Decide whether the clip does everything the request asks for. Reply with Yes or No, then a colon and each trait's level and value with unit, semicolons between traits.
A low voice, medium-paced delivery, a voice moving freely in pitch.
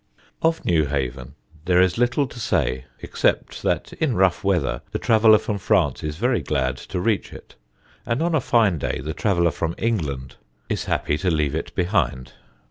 Yes: very low, 90 Hz; average, 175 wpm; wide, 6.9 semitones